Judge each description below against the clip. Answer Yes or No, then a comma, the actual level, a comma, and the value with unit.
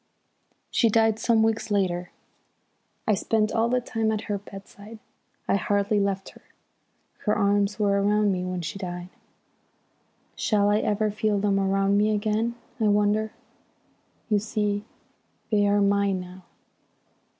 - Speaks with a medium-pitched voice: No, high, 205 Hz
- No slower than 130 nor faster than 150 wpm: Yes, average, 140 wpm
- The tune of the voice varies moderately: No, narrow, 1.4 semitones